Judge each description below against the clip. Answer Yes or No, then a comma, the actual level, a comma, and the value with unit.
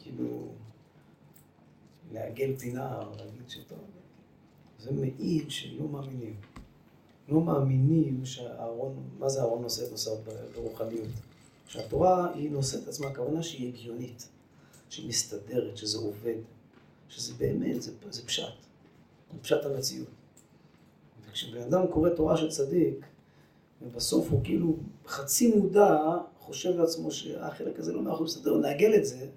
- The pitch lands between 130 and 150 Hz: Yes, low, 135 Hz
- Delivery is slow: No, average, 120 wpm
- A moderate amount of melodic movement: No, wide, 5.7 semitones